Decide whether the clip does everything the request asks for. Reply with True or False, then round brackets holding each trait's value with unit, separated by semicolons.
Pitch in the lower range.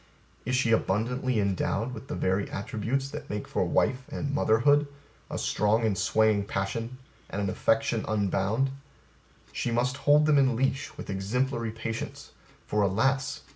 True (115 Hz)